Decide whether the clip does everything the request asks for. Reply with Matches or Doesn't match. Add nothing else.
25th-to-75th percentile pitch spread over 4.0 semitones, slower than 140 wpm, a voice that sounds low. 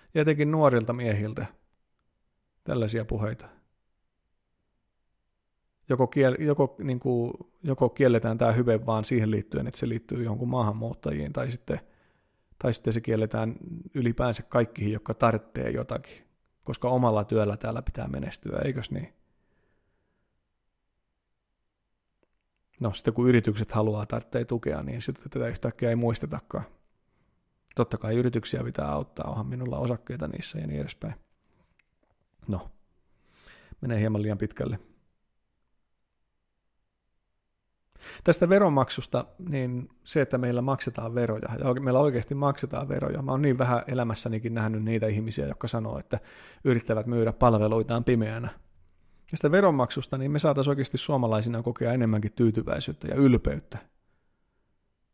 Doesn't match